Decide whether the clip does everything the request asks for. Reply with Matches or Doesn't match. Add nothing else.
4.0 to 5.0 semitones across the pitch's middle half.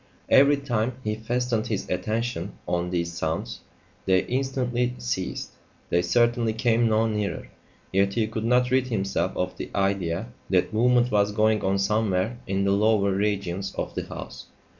Doesn't match